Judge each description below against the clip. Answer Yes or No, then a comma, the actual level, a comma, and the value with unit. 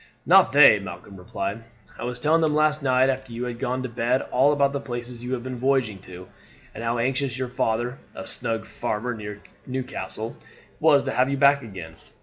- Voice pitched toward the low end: Yes, low, 125 Hz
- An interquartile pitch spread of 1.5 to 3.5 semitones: Yes, average, 2.9 semitones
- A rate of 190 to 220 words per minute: Yes, average, 200 wpm